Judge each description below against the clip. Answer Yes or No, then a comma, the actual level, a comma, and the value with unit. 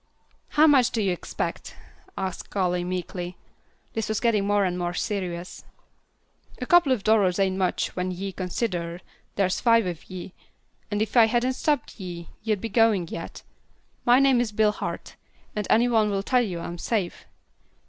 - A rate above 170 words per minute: No, average, 165 wpm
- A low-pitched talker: No, high, 200 Hz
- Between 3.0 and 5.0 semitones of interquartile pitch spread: Yes, average, 4.0 semitones